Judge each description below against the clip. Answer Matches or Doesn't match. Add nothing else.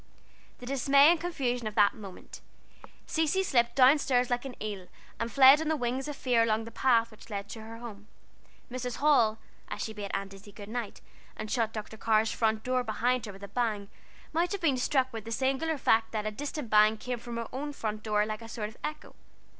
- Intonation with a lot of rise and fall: Doesn't match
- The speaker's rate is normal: Doesn't match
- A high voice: Matches